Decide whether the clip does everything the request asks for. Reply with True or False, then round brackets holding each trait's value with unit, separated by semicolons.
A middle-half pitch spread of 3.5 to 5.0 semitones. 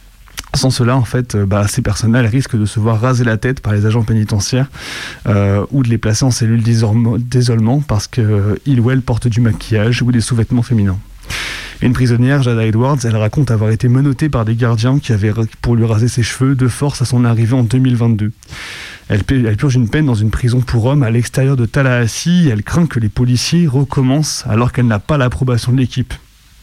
False (2.7 semitones)